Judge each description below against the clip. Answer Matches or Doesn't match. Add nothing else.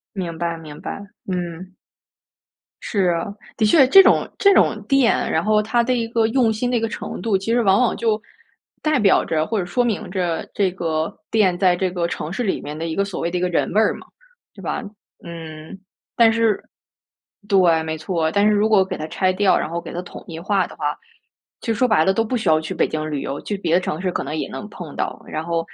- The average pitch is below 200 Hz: Matches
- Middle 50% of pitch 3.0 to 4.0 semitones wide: Doesn't match